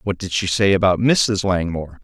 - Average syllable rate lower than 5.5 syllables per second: Yes, 5.1 syllables/s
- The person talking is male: Yes, male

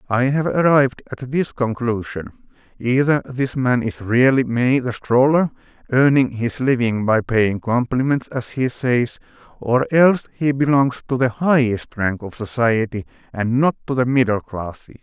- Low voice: Yes, low, 125 Hz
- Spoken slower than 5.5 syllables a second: Yes, 4.5 syllables/s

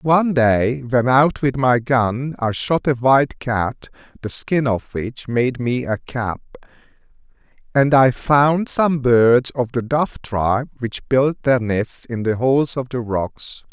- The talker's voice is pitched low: Yes, low, 125 Hz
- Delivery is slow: No, average, 165 wpm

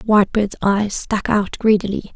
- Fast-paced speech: No, average, 140 wpm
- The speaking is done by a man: No, female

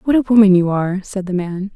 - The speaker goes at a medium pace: No, fast, 275 wpm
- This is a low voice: No, high, 195 Hz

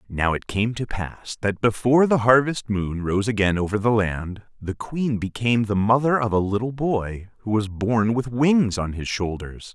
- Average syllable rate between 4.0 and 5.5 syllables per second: Yes, 4.6 syllables/s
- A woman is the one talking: No, male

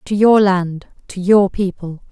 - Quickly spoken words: No, average, 140 wpm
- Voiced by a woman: Yes, female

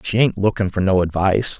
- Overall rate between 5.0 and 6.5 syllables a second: Yes, 6.0 syllables/s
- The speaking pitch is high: No, low, 100 Hz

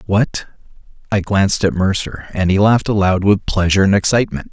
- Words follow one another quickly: No, average, 160 wpm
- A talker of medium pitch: No, low, 100 Hz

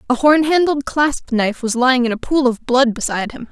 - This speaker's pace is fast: Yes, fast, 240 wpm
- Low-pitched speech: No, very high, 260 Hz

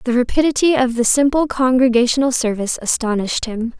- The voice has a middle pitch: No, very high, 250 Hz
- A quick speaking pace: No, average, 140 wpm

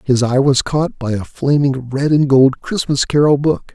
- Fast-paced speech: Yes, fast, 210 wpm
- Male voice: Yes, male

